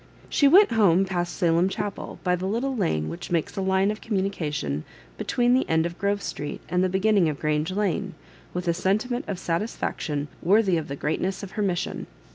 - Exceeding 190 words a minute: Yes, average, 200 wpm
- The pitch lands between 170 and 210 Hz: Yes, medium, 185 Hz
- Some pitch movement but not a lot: Yes, average, 3.7 semitones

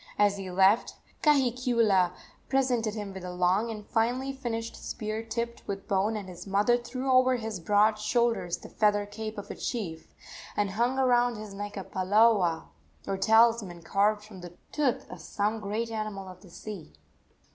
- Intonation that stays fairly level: No, average, 3.1 semitones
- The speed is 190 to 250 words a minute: No, average, 170 wpm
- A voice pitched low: No, high, 215 Hz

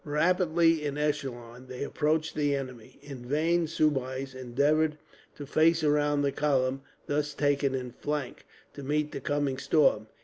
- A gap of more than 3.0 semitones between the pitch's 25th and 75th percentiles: No, narrow, 2.4 semitones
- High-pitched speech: No, medium, 145 Hz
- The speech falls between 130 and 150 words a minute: Yes, average, 145 wpm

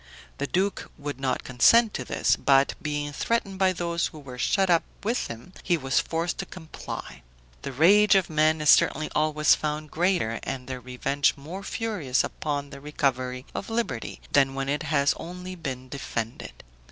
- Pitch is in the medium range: Yes, medium, 150 Hz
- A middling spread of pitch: Yes, average, 4.7 semitones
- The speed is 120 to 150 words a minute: No, average, 175 wpm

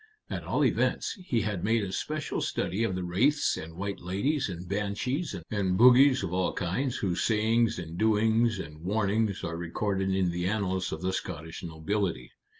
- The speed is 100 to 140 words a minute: No, average, 175 wpm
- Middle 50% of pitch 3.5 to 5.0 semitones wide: Yes, average, 3.9 semitones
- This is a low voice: Yes, low, 100 Hz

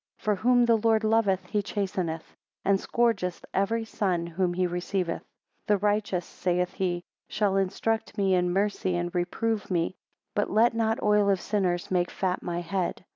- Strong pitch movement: No, average, 2.9 semitones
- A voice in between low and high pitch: No, high, 195 Hz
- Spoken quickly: No, average, 170 wpm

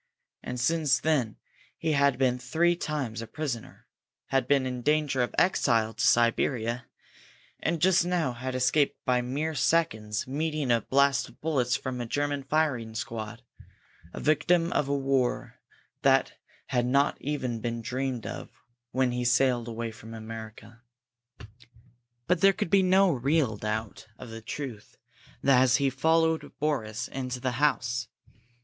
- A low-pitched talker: Yes, low, 130 Hz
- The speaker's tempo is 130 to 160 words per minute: Yes, average, 150 wpm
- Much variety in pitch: No, average, 4.1 semitones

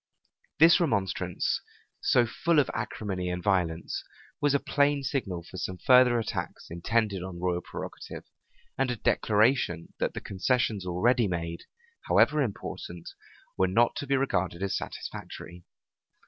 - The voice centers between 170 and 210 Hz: No, low, 100 Hz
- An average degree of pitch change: No, wide, 6.3 semitones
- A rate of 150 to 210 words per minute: No, average, 140 wpm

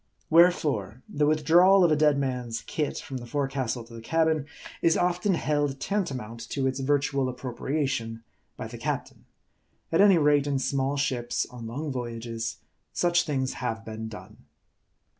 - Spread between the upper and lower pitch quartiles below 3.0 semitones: No, average, 4.2 semitones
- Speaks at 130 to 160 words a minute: Yes, average, 155 wpm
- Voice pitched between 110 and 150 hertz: Yes, low, 135 Hz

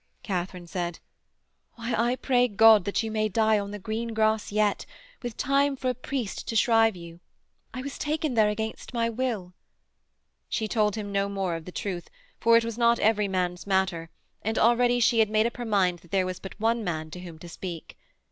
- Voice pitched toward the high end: Yes, high, 215 Hz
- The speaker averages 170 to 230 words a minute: Yes, fast, 205 wpm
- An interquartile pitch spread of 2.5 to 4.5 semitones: Yes, average, 3.7 semitones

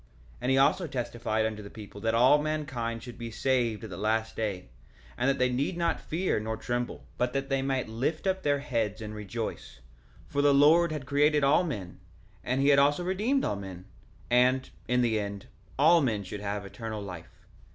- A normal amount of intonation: Yes, average, 4.8 semitones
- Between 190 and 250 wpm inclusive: Yes, average, 200 wpm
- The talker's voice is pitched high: No, low, 125 Hz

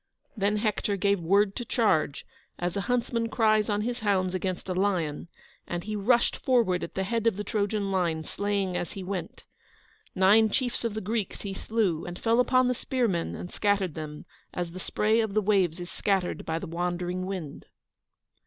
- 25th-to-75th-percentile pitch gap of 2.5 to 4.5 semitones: Yes, average, 3.4 semitones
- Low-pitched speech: No, high, 200 Hz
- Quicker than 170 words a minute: Yes, average, 190 wpm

